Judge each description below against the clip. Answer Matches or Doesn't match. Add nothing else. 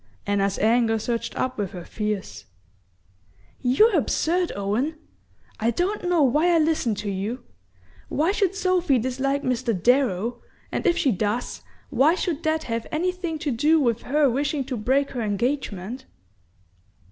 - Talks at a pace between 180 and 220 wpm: Doesn't match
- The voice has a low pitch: Doesn't match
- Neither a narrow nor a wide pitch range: Doesn't match